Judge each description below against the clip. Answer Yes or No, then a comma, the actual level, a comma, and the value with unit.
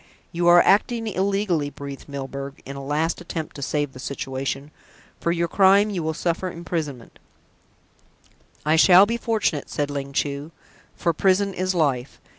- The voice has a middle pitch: Yes, medium, 160 Hz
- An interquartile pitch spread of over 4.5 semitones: Yes, average, 4.9 semitones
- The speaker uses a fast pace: No, average, 155 wpm